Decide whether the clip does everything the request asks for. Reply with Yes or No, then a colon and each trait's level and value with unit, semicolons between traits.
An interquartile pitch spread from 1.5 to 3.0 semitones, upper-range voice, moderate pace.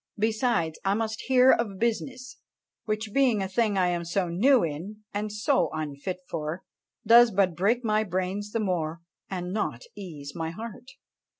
No: average, 4.4 semitones; high, 205 Hz; average, 165 wpm